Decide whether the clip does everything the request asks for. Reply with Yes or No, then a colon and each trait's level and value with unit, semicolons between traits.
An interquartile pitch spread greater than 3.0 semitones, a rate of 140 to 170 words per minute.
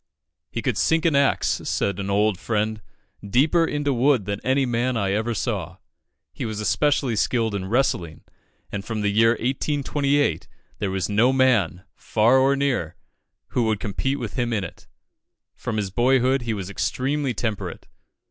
Yes: average, 4.6 semitones; average, 165 wpm